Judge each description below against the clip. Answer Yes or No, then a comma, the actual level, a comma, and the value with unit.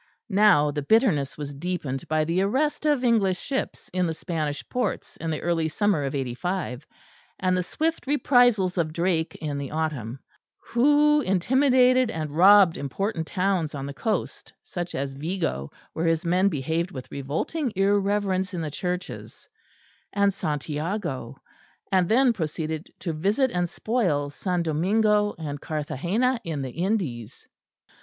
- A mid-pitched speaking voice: Yes, medium, 175 Hz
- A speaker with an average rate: Yes, average, 145 wpm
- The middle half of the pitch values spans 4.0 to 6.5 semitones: Yes, wide, 5.4 semitones